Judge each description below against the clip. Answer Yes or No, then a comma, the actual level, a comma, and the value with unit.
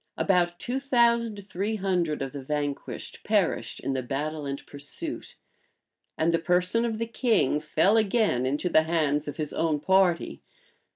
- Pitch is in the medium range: Yes, medium, 170 Hz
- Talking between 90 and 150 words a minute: No, average, 160 wpm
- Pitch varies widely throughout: Yes, wide, 6.4 semitones